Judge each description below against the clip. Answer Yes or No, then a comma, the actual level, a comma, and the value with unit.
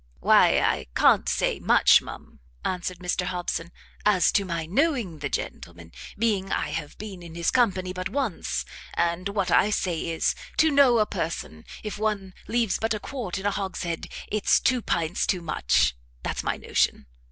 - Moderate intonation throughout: Yes, average, 4.0 semitones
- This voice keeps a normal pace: Yes, average, 175 wpm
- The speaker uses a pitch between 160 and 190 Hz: Yes, medium, 185 Hz